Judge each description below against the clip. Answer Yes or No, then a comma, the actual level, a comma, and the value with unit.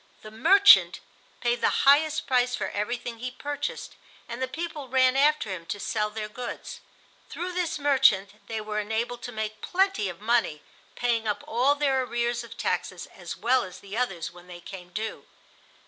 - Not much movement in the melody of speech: No, average, 4.2 semitones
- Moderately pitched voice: No, high, 240 Hz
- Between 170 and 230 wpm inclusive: Yes, average, 180 wpm